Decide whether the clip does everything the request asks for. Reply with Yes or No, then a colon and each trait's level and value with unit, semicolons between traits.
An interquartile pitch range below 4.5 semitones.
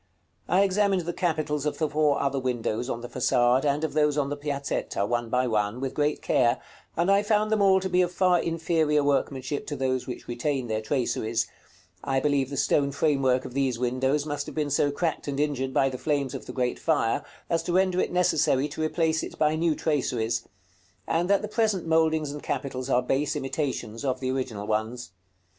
Yes: average, 3.9 semitones